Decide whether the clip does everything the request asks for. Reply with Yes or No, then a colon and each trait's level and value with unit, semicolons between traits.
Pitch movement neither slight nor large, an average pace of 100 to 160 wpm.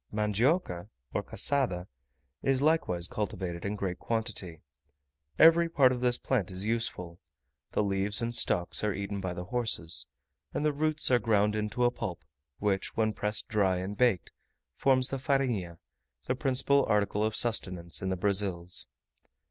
Yes: average, 5.0 semitones; average, 155 wpm